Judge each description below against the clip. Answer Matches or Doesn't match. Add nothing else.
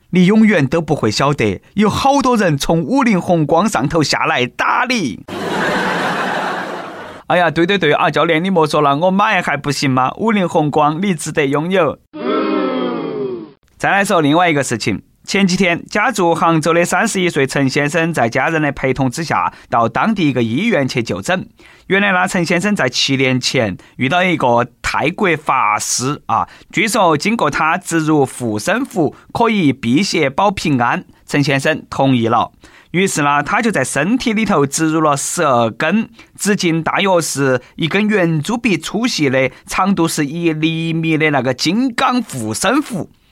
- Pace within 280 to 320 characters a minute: Doesn't match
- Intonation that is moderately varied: Doesn't match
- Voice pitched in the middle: Matches